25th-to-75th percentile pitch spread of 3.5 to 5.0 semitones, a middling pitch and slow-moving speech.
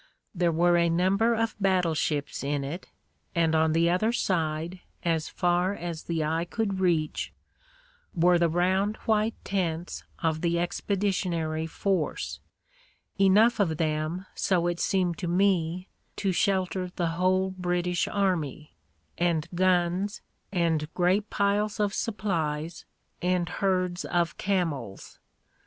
No: average, 2.7 semitones; medium, 175 Hz; slow, 130 wpm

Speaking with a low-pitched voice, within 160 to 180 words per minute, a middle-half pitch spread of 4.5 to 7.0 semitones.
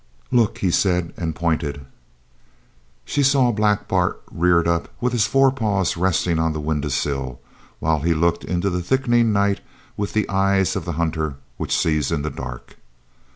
Yes: very low, 85 Hz; average, 165 wpm; average, 4.8 semitones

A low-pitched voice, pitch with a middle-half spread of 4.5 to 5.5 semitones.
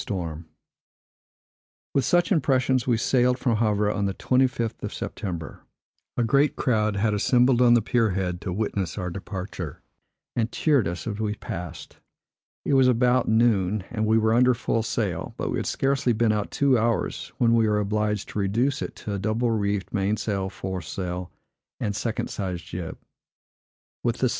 No: low, 110 Hz; average, 3.7 semitones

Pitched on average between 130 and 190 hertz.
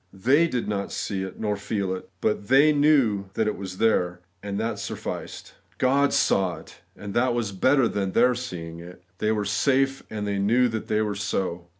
No: low, 105 Hz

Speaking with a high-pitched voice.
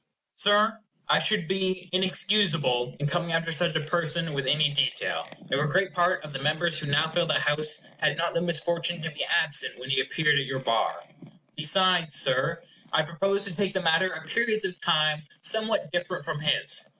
No: medium, 165 Hz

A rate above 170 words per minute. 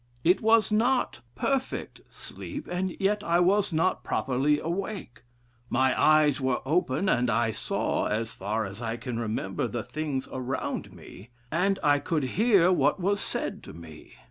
No: average, 160 wpm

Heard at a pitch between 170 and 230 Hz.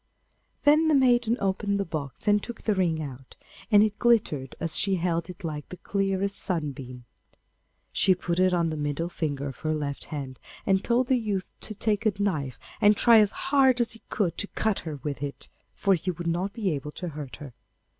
Yes: medium, 185 Hz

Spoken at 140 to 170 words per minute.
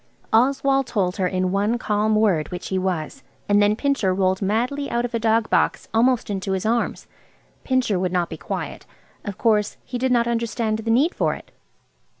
No: average, 190 wpm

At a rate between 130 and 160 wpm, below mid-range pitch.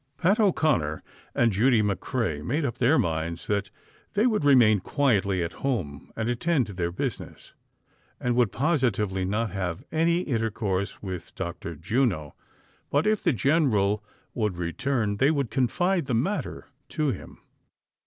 Yes: average, 155 wpm; low, 115 Hz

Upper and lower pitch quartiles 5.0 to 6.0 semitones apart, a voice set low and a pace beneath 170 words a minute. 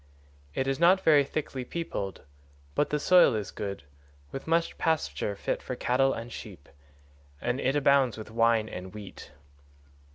Yes: average, 5.3 semitones; low, 130 Hz; average, 160 wpm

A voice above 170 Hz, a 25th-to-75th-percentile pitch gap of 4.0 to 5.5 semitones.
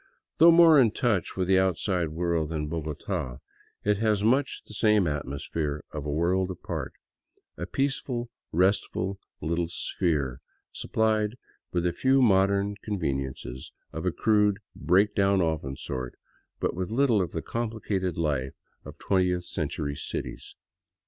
No: very low, 95 Hz; average, 5.1 semitones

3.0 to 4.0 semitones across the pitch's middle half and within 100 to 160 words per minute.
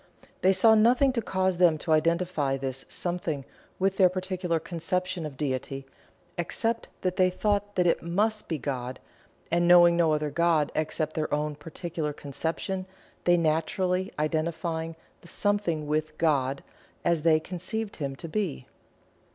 Yes: average, 3.4 semitones; average, 150 wpm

